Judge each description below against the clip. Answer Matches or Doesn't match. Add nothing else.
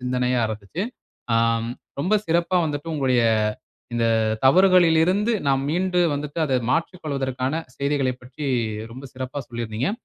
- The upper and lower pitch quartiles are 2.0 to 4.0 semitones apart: Doesn't match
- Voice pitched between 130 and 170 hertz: Matches